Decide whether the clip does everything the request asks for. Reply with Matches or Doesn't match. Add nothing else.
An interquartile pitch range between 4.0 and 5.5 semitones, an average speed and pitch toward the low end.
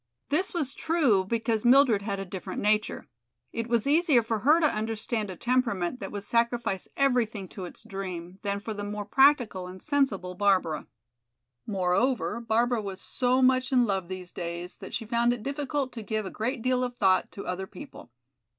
Doesn't match